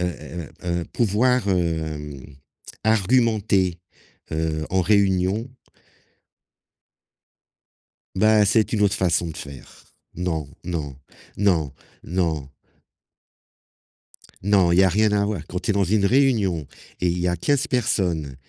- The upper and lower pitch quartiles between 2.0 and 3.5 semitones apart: No, average, 4.0 semitones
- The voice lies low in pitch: Yes, very low, 95 Hz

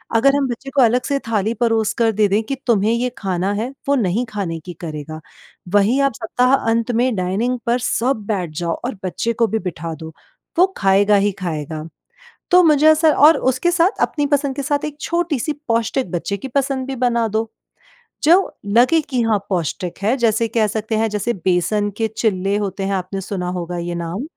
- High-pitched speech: Yes, high, 225 Hz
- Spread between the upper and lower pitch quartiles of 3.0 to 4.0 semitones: No, average, 5.2 semitones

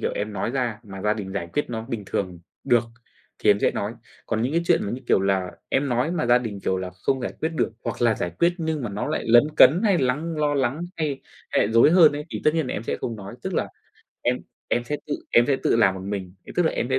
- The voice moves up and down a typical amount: No, wide, 6.3 semitones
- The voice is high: No, low, 120 Hz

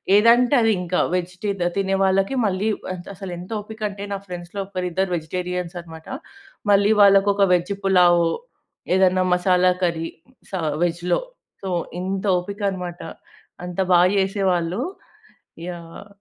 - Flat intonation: Yes, narrow, 2.0 semitones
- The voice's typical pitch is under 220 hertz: Yes, medium, 185 Hz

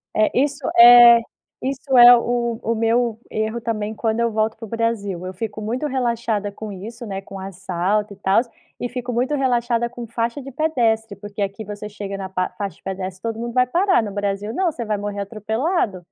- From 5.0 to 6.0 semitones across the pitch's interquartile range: No, average, 2.9 semitones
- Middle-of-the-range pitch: No, high, 225 Hz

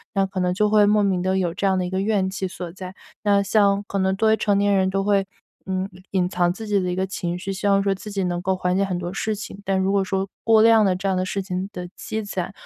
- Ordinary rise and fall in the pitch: No, narrow, 1.5 semitones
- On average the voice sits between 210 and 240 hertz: No, high, 195 Hz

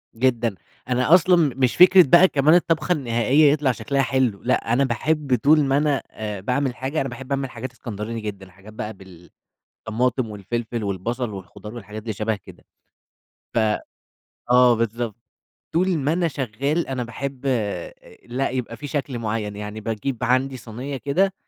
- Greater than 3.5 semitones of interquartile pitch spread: Yes, average, 3.9 semitones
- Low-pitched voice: Yes, low, 125 Hz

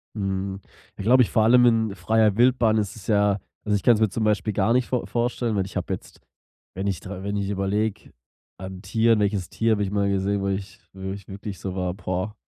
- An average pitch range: No, narrow, 2.3 semitones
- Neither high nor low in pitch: No, low, 100 Hz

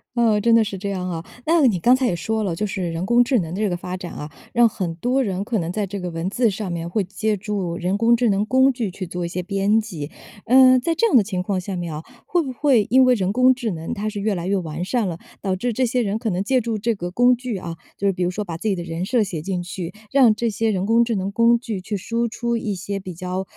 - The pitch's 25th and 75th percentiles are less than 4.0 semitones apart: No, average, 4.4 semitones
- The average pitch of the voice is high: Yes, high, 205 Hz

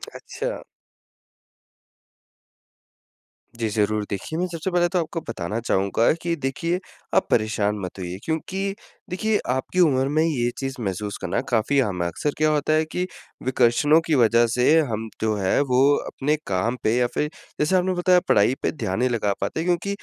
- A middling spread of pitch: No, wide, 7.2 semitones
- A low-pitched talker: Yes, low, 130 Hz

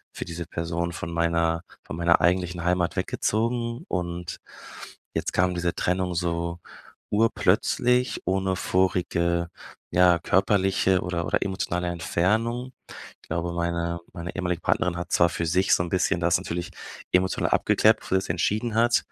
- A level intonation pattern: Yes, narrow, 1.8 semitones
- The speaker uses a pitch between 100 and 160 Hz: No, very low, 90 Hz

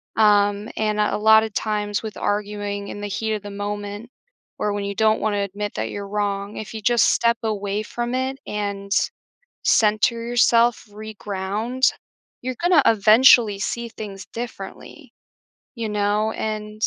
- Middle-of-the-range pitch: No, high, 210 Hz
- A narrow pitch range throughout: Yes, narrow, 1.5 semitones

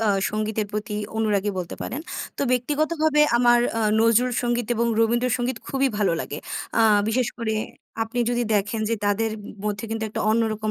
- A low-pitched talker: No, high, 225 Hz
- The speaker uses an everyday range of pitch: No, narrow, 2.3 semitones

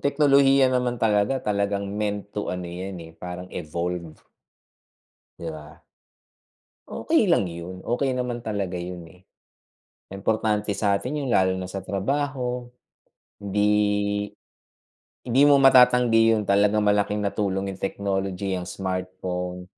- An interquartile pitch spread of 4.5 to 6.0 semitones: No, average, 3.9 semitones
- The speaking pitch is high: No, low, 100 Hz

